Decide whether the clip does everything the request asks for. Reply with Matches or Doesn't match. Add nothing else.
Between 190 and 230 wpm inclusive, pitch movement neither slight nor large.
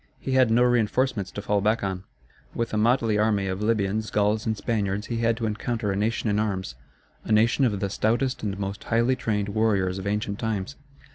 Doesn't match